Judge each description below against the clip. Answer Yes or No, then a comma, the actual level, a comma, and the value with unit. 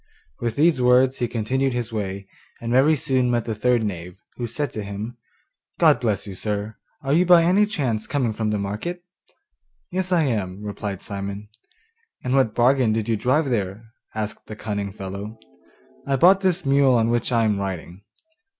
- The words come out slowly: No, average, 180 wpm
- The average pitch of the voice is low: Yes, low, 115 Hz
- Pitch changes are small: No, average, 4.5 semitones